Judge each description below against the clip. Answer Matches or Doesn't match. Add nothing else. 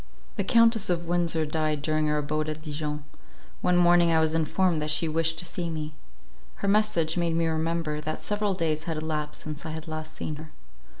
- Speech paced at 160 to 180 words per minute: Doesn't match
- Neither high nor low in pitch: Matches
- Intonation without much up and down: Matches